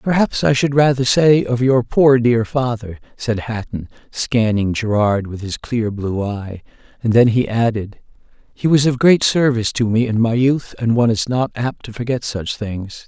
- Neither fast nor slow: Yes, average, 195 wpm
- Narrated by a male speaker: Yes, male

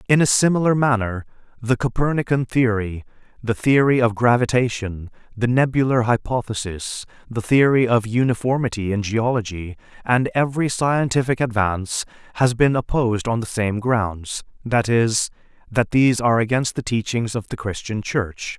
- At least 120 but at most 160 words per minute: Yes, average, 140 wpm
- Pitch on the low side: Yes, low, 120 Hz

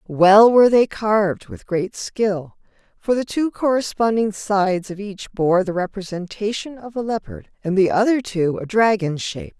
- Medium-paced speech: Yes, average, 170 wpm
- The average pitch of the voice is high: Yes, high, 205 Hz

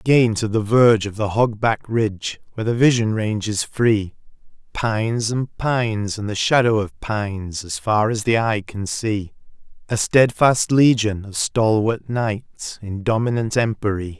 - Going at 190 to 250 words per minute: No, average, 160 wpm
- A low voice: Yes, low, 110 Hz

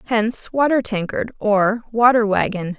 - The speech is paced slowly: Yes, slow, 130 wpm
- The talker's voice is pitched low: No, high, 220 Hz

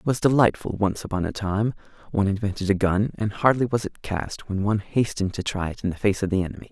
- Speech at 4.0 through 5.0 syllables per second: No, 6.4 syllables/s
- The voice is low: Yes, low, 105 Hz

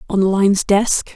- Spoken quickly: No, average, 155 wpm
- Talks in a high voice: Yes, high, 200 Hz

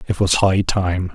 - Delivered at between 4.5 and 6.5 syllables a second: No, 4.0 syllables/s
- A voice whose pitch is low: Yes, very low, 90 Hz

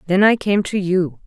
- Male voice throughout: No, female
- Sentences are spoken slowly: No, fast, 235 wpm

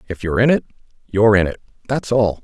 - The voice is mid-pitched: No, low, 110 Hz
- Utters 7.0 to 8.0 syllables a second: Yes, 7.2 syllables/s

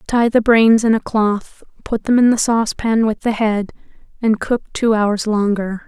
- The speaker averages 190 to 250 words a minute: Yes, average, 195 wpm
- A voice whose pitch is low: No, high, 220 Hz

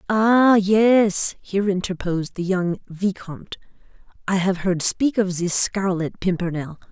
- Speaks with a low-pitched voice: No, high, 190 Hz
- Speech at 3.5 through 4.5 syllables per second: Yes, 4.1 syllables/s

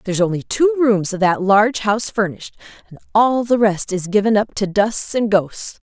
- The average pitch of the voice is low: No, high, 205 Hz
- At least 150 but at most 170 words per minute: No, fast, 205 wpm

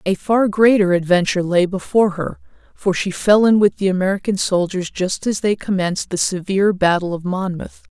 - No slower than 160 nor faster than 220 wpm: Yes, average, 180 wpm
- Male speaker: No, female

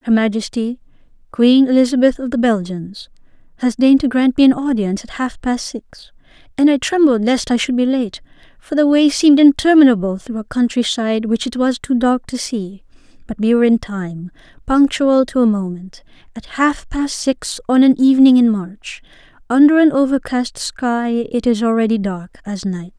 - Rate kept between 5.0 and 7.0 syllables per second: Yes, 5.1 syllables/s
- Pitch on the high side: Yes, high, 240 Hz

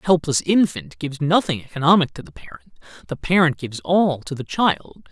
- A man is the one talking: Yes, male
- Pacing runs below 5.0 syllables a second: No, 5.5 syllables/s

